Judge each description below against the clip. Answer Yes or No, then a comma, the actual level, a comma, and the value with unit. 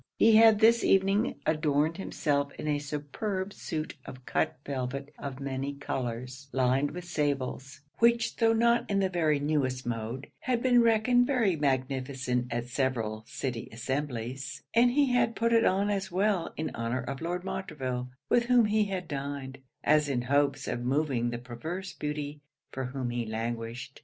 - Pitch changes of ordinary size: No, wide, 7.0 semitones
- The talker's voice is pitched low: No, medium, 145 Hz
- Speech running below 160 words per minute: No, average, 165 wpm